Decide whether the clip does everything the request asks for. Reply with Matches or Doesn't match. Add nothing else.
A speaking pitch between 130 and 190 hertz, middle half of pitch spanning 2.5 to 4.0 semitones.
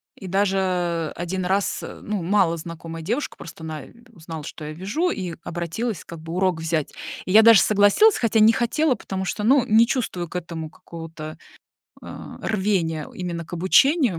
Doesn't match